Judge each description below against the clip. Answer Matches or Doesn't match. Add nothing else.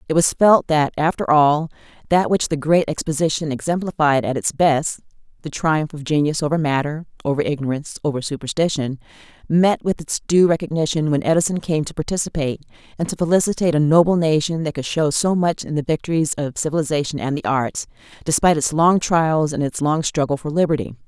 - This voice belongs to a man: Doesn't match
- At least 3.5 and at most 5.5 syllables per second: Doesn't match